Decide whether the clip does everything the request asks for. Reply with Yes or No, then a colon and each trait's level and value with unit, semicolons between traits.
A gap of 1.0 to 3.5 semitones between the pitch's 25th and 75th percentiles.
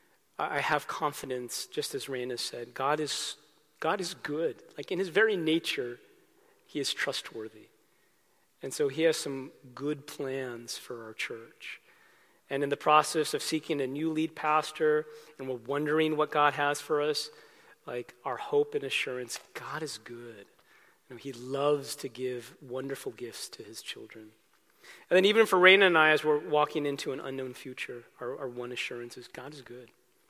No: average, 4.1 semitones